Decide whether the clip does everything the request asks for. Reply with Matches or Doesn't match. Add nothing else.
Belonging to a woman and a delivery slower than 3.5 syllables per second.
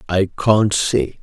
Doesn't match